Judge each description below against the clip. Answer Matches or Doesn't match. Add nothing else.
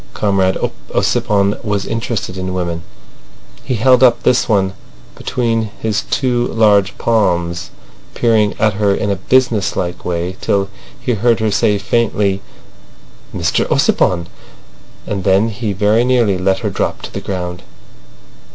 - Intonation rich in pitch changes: Doesn't match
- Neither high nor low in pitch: Doesn't match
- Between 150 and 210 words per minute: Doesn't match